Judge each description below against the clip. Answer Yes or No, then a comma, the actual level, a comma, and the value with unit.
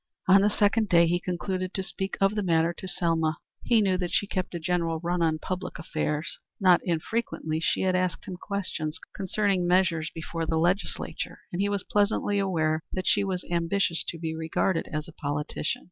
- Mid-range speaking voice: Yes, medium, 180 Hz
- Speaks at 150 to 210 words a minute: Yes, average, 190 wpm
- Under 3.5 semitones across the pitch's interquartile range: Yes, average, 2.8 semitones